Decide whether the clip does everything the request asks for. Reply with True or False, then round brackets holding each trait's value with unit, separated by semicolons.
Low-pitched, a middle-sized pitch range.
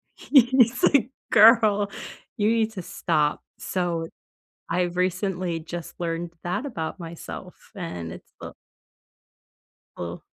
False (180 Hz; 4.5 semitones)